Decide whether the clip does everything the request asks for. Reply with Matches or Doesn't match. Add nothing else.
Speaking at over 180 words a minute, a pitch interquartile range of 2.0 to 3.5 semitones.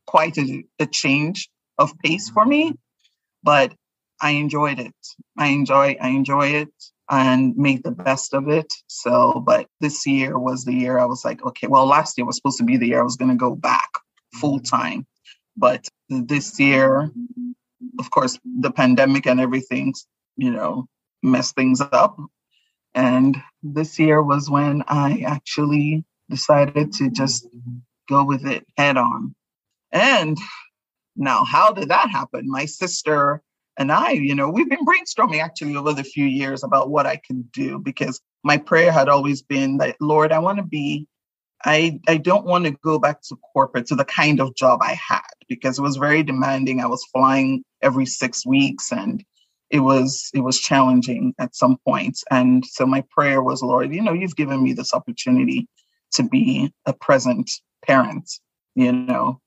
Doesn't match